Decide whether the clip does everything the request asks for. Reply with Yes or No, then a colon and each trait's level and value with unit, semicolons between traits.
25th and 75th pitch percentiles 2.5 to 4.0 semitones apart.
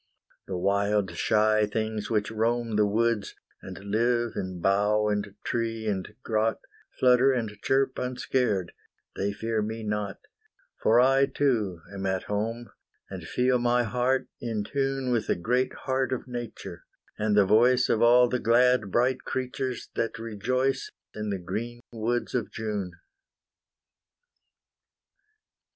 Yes: average, 3.1 semitones